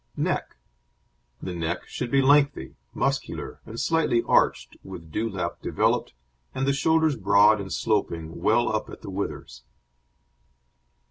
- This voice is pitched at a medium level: No, low, 110 Hz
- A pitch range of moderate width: No, wide, 6.9 semitones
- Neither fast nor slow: No, slow, 130 wpm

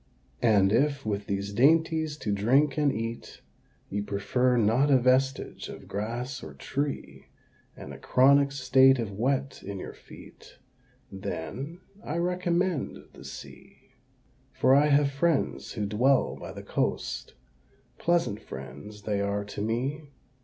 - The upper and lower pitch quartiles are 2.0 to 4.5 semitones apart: No, wide, 5.4 semitones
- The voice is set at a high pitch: No, low, 130 Hz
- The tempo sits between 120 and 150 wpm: Yes, average, 140 wpm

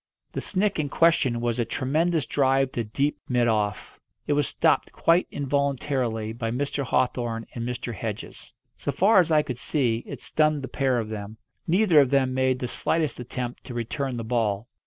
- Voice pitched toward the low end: Yes, low, 130 Hz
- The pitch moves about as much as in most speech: Yes, average, 3.7 semitones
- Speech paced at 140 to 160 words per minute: No, average, 185 wpm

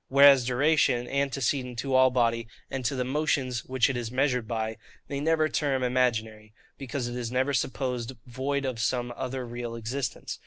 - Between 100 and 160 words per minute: No, average, 170 wpm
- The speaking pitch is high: No, low, 125 Hz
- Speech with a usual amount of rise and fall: No, narrow, 2.3 semitones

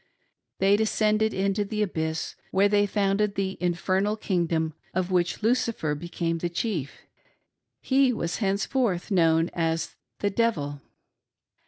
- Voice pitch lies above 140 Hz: Yes, high, 190 Hz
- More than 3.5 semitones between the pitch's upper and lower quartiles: Yes, average, 4.0 semitones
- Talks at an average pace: No, slow, 130 wpm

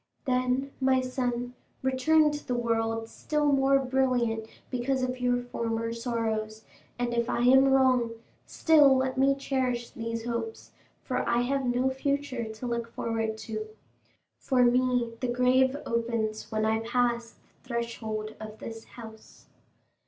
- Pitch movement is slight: Yes, narrow, 2.3 semitones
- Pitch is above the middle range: Yes, high, 245 Hz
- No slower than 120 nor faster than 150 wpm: Yes, average, 145 wpm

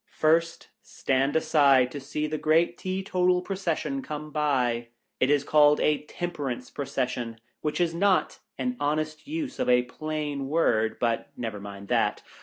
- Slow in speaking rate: No, average, 160 wpm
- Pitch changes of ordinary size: Yes, average, 4.3 semitones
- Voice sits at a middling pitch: Yes, medium, 150 Hz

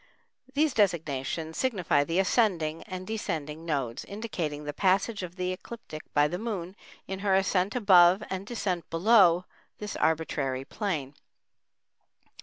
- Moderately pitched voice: Yes, medium, 180 Hz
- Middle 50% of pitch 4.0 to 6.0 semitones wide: Yes, average, 4.4 semitones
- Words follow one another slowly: Yes, slow, 130 wpm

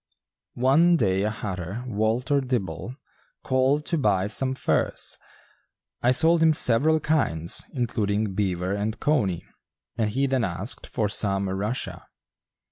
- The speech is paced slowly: Yes, slow, 125 wpm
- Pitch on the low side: Yes, low, 110 Hz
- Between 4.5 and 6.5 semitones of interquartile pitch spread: Yes, average, 5.2 semitones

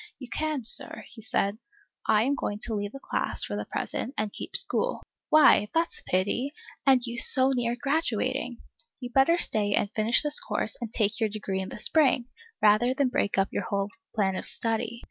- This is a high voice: Yes, high, 235 Hz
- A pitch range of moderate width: Yes, average, 4.2 semitones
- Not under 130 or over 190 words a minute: No, fast, 205 wpm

